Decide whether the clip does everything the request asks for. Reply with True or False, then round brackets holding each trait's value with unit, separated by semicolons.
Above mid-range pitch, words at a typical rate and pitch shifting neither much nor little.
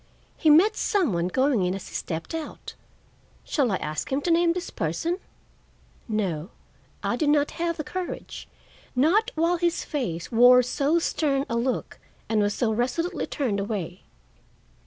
False (270 Hz; 160 wpm; 8.2 semitones)